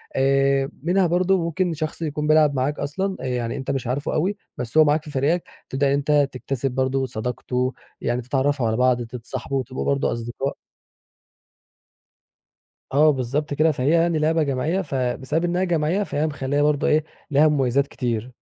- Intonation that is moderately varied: Yes, average, 3.3 semitones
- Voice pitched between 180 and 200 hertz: No, medium, 140 Hz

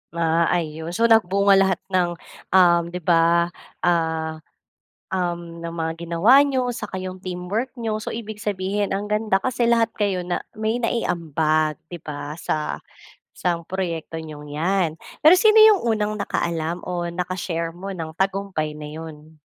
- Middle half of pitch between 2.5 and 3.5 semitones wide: No, average, 4.0 semitones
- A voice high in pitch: No, medium, 180 Hz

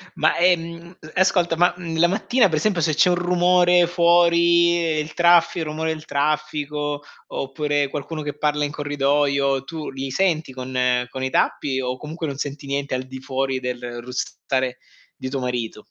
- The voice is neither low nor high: Yes, medium, 150 Hz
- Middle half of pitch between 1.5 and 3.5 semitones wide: No, average, 4.0 semitones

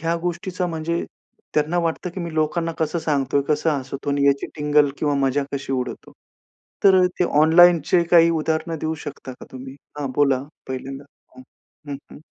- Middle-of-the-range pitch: Yes, medium, 155 Hz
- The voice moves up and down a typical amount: Yes, average, 3.3 semitones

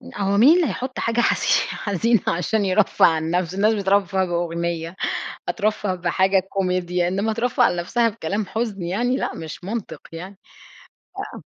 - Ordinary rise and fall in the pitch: Yes, average, 3.9 semitones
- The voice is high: Yes, high, 195 Hz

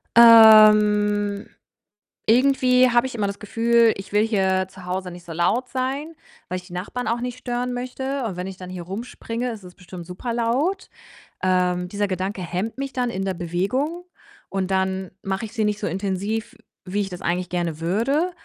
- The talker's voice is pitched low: No, high, 205 Hz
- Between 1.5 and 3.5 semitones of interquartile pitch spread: No, average, 4.5 semitones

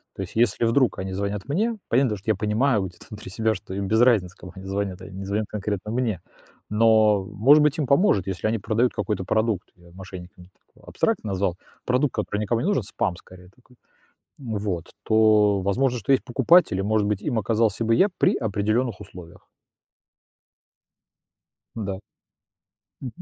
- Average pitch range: Yes, average, 3.5 semitones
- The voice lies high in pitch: No, low, 105 Hz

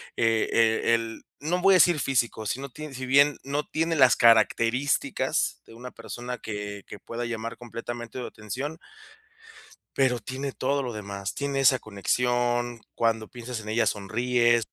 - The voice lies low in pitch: Yes, low, 120 Hz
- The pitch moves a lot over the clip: No, average, 3.1 semitones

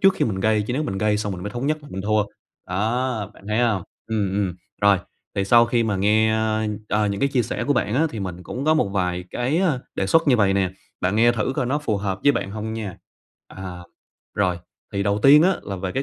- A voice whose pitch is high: No, low, 105 Hz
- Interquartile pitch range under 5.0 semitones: Yes, average, 3.8 semitones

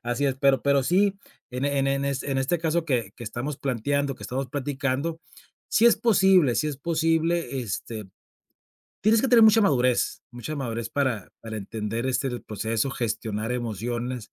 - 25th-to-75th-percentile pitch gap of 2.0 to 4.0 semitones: No, average, 4.6 semitones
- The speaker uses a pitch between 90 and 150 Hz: Yes, low, 135 Hz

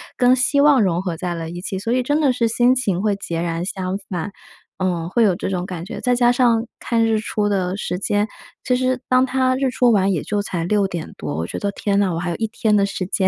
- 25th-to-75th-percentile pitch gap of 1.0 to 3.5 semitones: No, average, 5.2 semitones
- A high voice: Yes, high, 205 Hz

